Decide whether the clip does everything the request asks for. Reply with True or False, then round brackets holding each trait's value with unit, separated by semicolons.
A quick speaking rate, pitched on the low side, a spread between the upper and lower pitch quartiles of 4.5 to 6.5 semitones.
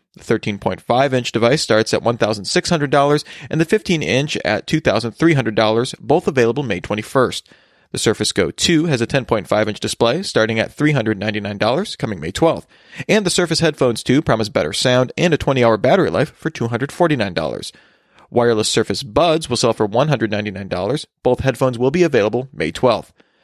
False (160 wpm; 125 Hz; 5.2 semitones)